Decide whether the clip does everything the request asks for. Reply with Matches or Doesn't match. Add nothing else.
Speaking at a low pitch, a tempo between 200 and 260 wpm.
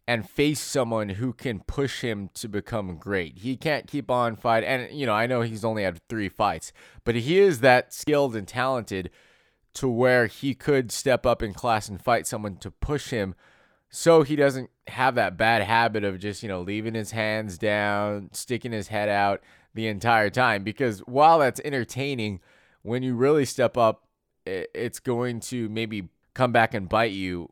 Doesn't match